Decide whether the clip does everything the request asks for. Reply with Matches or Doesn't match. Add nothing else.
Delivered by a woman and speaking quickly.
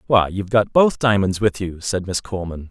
Doesn't match